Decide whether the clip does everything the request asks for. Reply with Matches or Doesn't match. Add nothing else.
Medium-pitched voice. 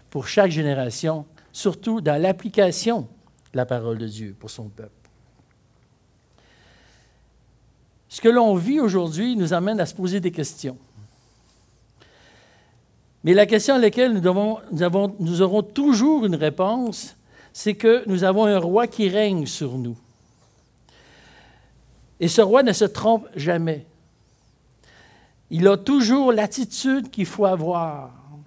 Matches